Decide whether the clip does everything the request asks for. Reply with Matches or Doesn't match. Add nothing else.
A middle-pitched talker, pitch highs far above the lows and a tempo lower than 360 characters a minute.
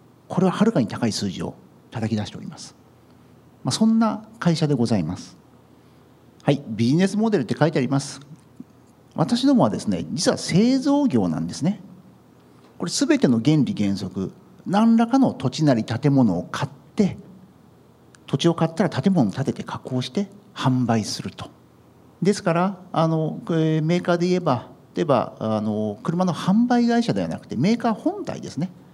Matches